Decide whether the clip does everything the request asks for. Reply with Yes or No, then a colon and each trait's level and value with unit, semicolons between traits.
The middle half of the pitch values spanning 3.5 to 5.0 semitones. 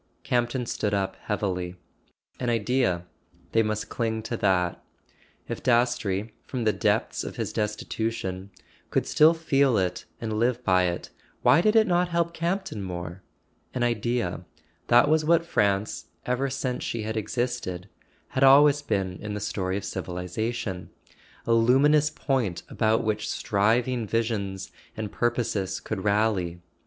Yes: average, 4.3 semitones